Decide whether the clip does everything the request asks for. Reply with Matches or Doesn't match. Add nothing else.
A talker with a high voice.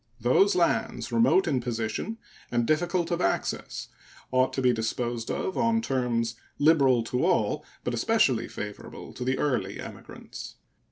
Doesn't match